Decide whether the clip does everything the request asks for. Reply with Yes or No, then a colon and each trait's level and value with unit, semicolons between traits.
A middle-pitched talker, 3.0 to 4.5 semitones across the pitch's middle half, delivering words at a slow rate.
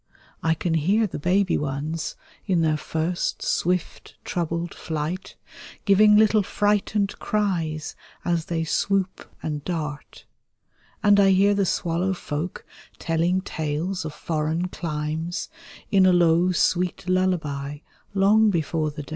Yes: medium, 175 Hz; average, 3.4 semitones; slow, 130 wpm